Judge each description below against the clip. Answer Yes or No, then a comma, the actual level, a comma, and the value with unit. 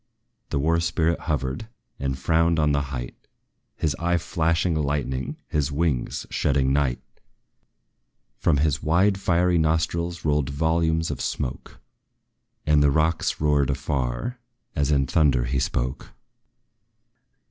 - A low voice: Yes, very low, 75 Hz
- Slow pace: Yes, slow, 125 wpm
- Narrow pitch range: No, average, 3.2 semitones